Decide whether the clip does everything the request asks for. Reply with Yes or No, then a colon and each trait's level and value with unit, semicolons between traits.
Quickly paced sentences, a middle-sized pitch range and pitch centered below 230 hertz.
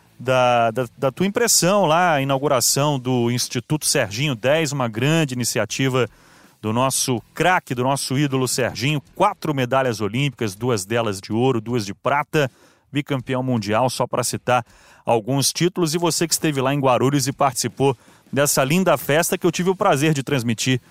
No: average, 165 wpm; average, 3.5 semitones; low, 135 Hz